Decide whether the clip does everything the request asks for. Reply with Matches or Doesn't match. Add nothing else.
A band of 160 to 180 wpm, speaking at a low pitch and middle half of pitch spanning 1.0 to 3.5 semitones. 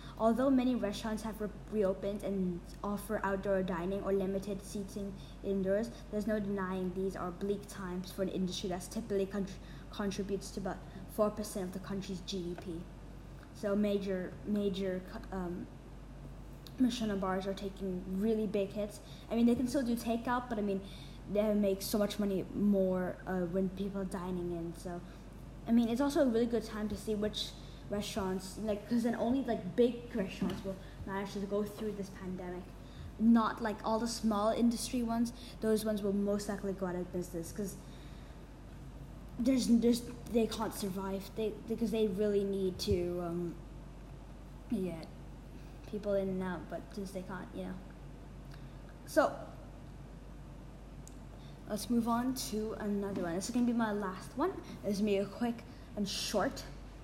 Doesn't match